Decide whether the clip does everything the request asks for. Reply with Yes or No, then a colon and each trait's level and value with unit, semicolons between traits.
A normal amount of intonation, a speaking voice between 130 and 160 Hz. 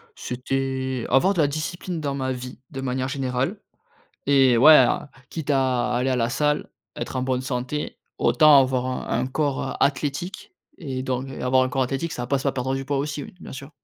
No: narrow, 2.1 semitones; low, 135 Hz